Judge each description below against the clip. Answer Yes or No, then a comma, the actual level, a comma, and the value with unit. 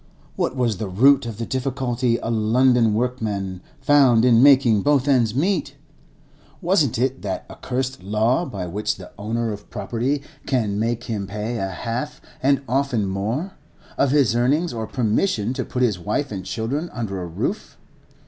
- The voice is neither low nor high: No, low, 120 Hz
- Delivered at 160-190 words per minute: Yes, average, 165 wpm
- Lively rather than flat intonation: No, average, 3.9 semitones